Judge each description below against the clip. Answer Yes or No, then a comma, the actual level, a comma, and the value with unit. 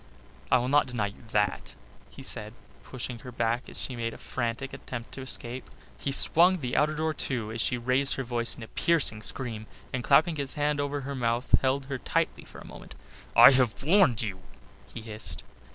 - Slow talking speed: No, average, 200 wpm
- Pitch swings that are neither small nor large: Yes, average, 3.2 semitones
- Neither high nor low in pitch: No, low, 125 Hz